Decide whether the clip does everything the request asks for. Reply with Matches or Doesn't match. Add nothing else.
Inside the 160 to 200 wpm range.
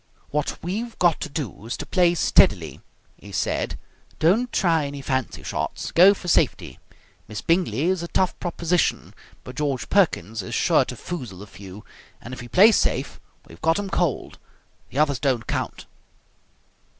Matches